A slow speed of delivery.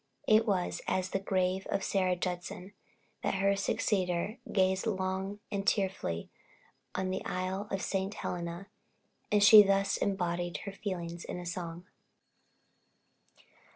Yes: slow, 125 wpm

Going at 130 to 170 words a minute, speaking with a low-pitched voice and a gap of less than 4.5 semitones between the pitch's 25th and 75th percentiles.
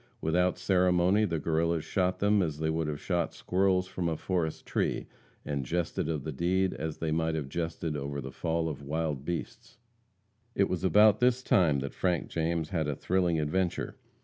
No: average, 185 wpm; very low, 85 Hz; average, 2.9 semitones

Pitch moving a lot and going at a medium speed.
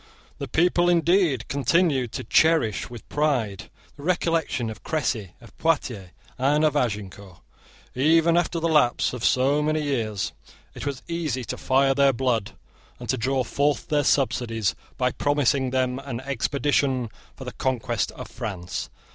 No: average, 4.1 semitones; average, 145 wpm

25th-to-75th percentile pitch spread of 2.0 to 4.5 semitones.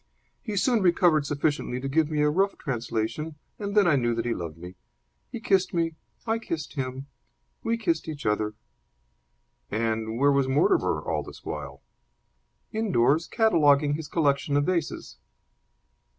No: wide, 5.6 semitones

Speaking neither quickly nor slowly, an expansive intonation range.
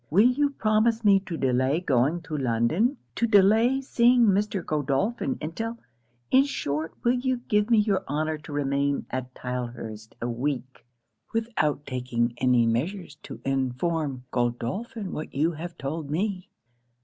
Yes: average, 150 wpm; wide, 8.7 semitones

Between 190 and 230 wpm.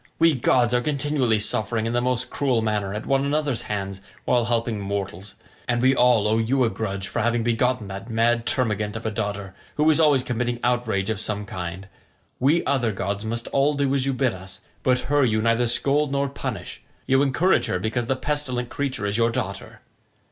Yes: average, 200 wpm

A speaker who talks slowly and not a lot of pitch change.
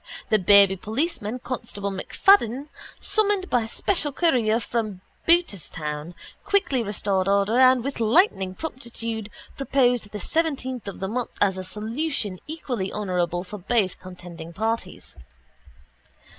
No: slow, 120 wpm; average, 5.3 semitones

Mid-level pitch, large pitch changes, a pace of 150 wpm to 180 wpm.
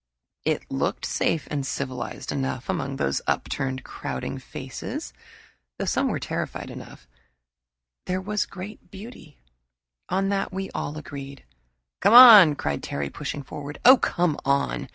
No: medium, 145 Hz; wide, 6.2 semitones; average, 140 wpm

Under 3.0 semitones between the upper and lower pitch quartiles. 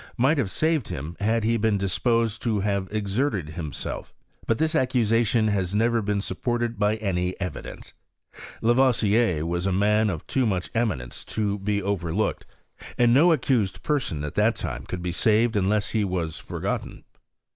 No: average, 3.7 semitones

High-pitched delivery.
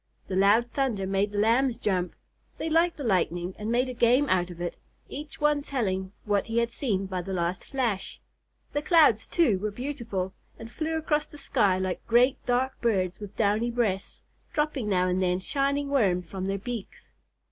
Yes: high, 225 Hz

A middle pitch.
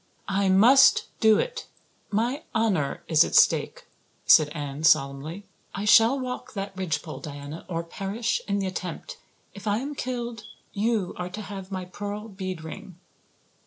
No: high, 195 Hz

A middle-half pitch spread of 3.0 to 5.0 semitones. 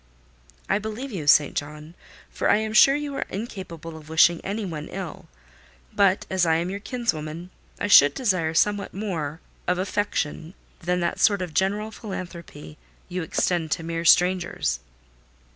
Yes: average, 4.0 semitones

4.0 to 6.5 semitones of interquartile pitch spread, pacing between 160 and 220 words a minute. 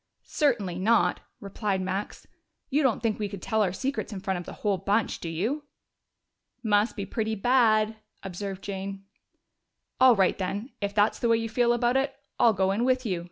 No: average, 3.4 semitones; average, 190 wpm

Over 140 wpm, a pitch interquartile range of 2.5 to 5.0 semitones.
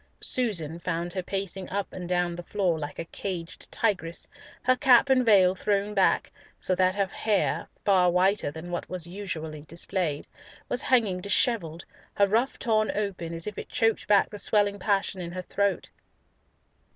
Yes: average, 165 wpm; average, 3.1 semitones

